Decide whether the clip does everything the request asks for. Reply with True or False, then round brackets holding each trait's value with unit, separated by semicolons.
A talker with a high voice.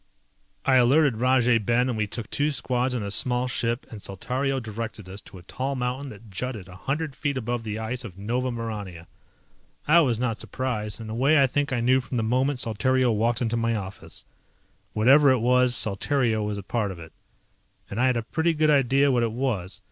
False (120 Hz)